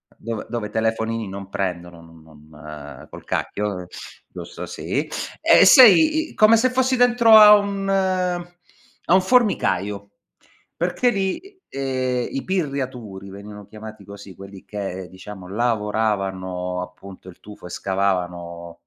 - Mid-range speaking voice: No, low, 105 Hz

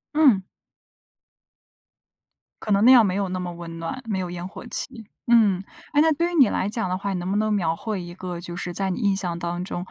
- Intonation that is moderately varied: Yes, average, 3.9 semitones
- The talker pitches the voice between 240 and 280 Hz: No, high, 190 Hz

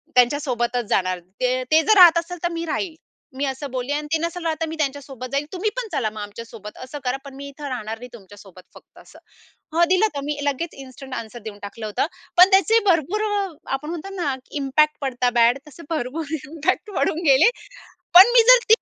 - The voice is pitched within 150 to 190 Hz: No, very high, 280 Hz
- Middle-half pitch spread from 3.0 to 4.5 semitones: No, average, 5.0 semitones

